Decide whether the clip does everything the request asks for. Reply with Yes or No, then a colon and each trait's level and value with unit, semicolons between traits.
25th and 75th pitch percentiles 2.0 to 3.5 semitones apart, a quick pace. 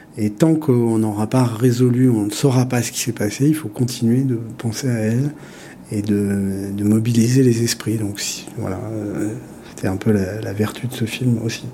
No: average, 2.8 semitones; average, 200 wpm